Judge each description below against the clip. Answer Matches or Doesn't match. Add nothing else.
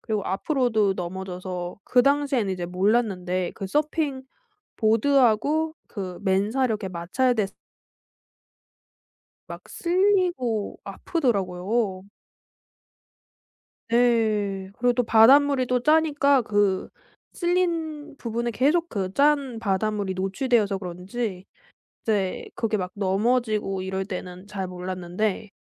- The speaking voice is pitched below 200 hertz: Doesn't match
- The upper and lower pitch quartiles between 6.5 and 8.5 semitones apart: Doesn't match